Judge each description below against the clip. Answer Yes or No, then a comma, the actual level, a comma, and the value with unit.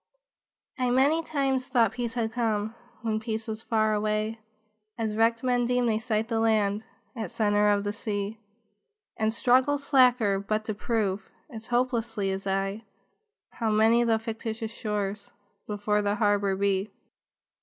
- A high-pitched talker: Yes, high, 220 Hz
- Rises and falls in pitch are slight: Yes, narrow, 2.2 semitones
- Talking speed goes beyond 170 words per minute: No, average, 150 wpm